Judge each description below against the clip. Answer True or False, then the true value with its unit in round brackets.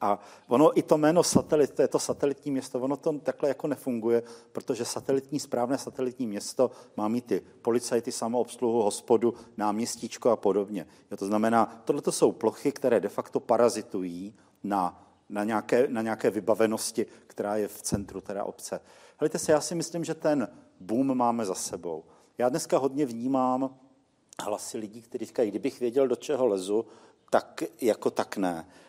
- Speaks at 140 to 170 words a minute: True (165 wpm)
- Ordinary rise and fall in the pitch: True (3.4 semitones)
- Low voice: True (120 Hz)